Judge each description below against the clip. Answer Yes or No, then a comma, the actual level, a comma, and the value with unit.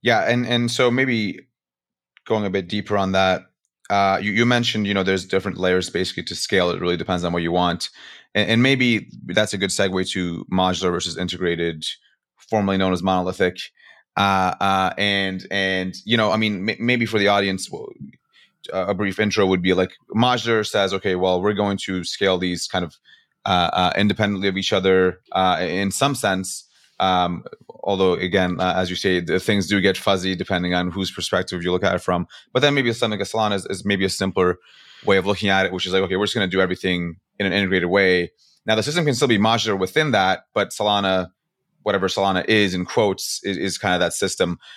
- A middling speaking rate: No, fast, 210 wpm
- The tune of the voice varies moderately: No, narrow, 2.2 semitones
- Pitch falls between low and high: No, very low, 95 Hz